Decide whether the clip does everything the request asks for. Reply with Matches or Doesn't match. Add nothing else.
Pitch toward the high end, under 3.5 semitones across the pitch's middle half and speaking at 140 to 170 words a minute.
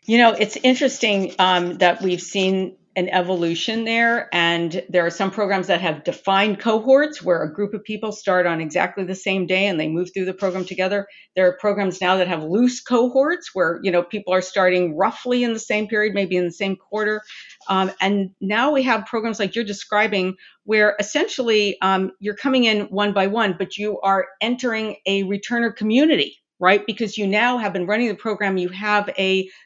Doesn't match